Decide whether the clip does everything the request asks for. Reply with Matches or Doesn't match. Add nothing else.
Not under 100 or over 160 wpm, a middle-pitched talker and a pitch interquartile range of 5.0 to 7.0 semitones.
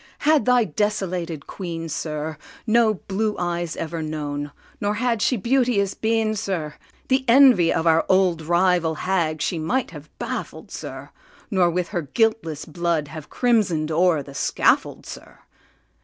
Matches